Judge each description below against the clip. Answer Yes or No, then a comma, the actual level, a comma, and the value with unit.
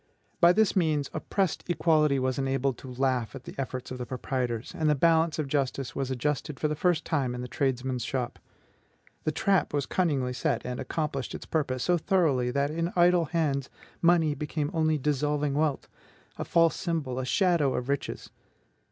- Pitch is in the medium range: Yes, medium, 145 Hz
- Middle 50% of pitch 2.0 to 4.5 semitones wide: Yes, average, 3.8 semitones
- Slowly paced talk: No, average, 180 wpm